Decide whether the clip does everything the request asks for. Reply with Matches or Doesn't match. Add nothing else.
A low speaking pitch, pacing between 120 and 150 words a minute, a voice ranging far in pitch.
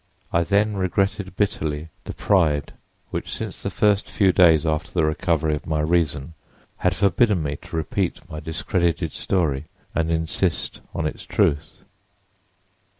Doesn't match